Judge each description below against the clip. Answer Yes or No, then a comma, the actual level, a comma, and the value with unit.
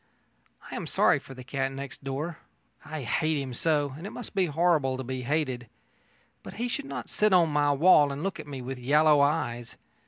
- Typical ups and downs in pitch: Yes, average, 3.4 semitones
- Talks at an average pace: No, fast, 210 wpm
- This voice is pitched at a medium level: Yes, medium, 145 Hz